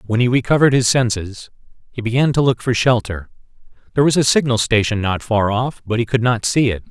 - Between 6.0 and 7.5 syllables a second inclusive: Yes, 6.1 syllables/s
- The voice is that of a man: Yes, male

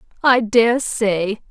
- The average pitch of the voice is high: Yes, high, 225 Hz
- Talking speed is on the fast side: No, slow, 120 wpm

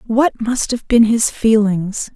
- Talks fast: No, average, 165 wpm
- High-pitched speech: Yes, high, 225 Hz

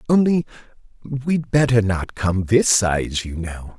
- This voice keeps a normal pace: Yes, average, 145 wpm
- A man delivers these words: Yes, male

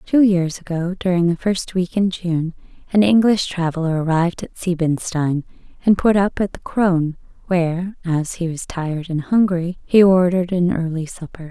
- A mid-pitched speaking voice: Yes, medium, 175 Hz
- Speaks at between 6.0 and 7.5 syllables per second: No, 5.0 syllables/s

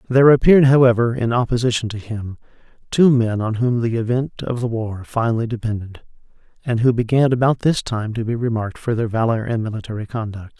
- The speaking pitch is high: No, low, 115 Hz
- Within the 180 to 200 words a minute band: Yes, average, 185 wpm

